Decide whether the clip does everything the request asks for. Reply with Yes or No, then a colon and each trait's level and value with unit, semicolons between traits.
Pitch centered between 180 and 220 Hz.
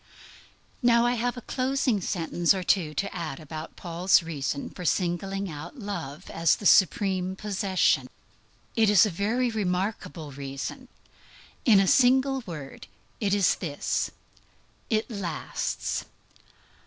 Yes: high, 190 Hz